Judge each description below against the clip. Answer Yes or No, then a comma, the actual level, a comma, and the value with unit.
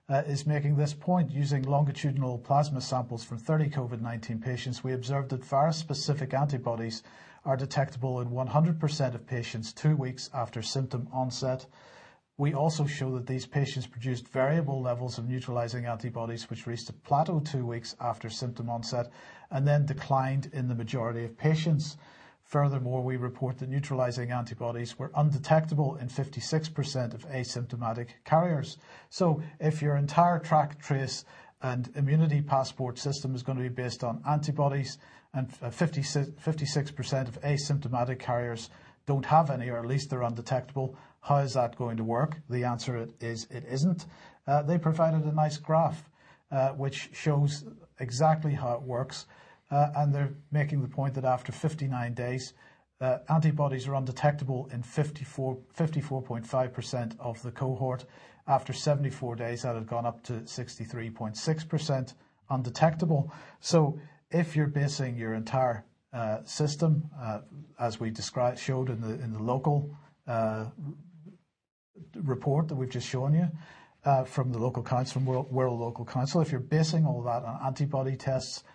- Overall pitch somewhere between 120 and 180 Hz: Yes, low, 135 Hz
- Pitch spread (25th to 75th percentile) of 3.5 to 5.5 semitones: No, average, 3.0 semitones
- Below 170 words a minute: Yes, average, 155 wpm